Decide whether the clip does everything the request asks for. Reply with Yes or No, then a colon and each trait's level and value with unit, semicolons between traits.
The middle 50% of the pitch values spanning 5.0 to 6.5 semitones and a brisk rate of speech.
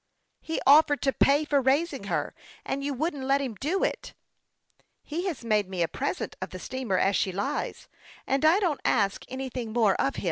Yes: wide, 5.4 semitones; fast, 215 wpm